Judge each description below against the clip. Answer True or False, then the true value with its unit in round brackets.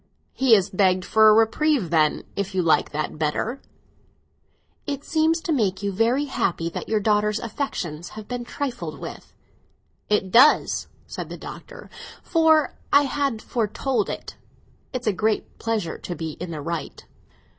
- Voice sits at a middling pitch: False (215 Hz)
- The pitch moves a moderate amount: False (6.6 semitones)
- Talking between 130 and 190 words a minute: True (155 wpm)